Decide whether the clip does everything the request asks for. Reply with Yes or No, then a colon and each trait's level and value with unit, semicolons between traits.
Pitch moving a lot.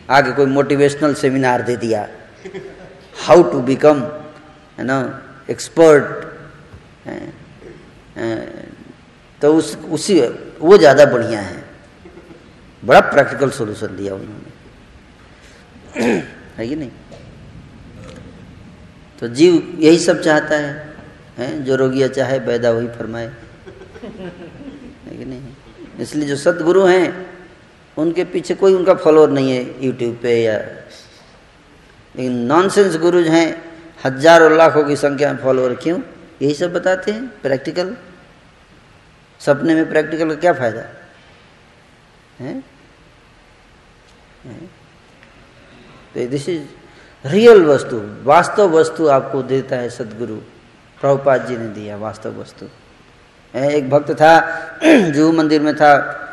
No: average, 4.4 semitones